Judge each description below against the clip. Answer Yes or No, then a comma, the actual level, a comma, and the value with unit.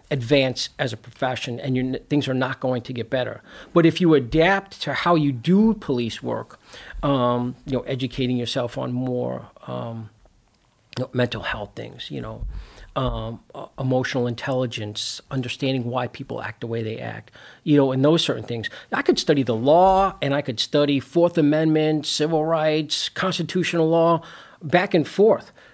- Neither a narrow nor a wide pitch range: Yes, average, 4.3 semitones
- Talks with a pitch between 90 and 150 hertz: Yes, low, 135 Hz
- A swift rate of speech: No, average, 175 wpm